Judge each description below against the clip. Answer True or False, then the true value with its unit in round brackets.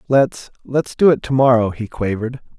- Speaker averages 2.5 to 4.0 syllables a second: False (5.1 syllables/s)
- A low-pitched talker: True (125 Hz)